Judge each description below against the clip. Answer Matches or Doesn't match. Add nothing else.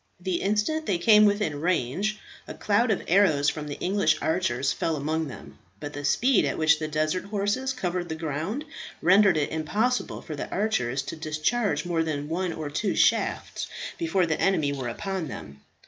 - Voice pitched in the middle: Matches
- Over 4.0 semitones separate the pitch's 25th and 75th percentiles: Matches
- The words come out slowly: Doesn't match